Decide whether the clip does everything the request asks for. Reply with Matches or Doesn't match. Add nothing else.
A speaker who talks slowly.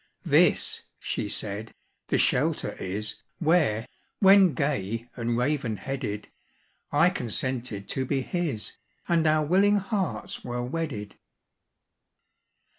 Matches